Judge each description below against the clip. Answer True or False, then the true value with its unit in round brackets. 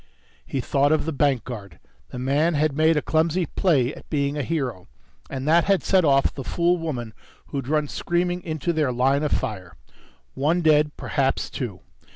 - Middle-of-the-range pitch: True (145 Hz)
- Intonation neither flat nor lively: True (3.5 semitones)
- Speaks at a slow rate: False (185 wpm)